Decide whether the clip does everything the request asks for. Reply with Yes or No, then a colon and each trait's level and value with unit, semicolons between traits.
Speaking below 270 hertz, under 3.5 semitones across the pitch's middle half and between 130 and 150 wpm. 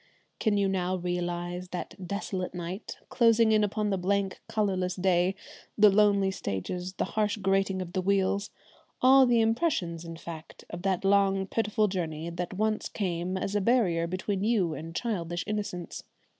No: high, 190 Hz; average, 2.8 semitones; average, 160 wpm